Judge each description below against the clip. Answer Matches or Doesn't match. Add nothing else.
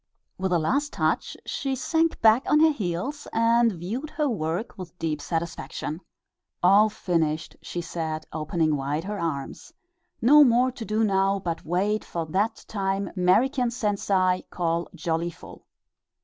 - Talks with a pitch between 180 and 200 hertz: Matches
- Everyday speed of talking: Matches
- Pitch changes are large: Matches